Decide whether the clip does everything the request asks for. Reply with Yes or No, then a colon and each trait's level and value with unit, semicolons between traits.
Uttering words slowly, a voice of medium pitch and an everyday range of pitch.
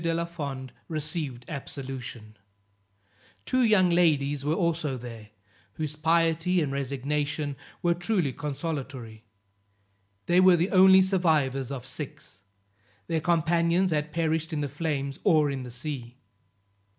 Yes: slow, 125 wpm; medium, 150 Hz; average, 3.7 semitones